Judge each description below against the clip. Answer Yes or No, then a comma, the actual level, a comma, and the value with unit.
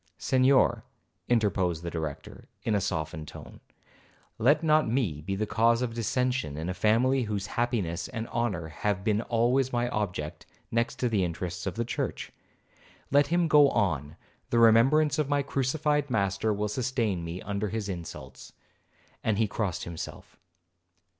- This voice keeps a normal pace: Yes, average, 155 wpm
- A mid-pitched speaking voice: No, low, 110 Hz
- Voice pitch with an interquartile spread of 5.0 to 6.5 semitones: Yes, wide, 5.4 semitones